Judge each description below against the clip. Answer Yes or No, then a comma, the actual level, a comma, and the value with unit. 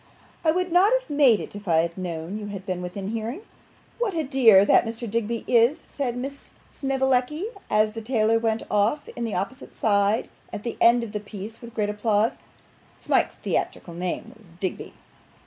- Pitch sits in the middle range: No, high, 225 Hz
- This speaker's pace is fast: No, average, 185 wpm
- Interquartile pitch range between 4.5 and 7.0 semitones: No, average, 4.1 semitones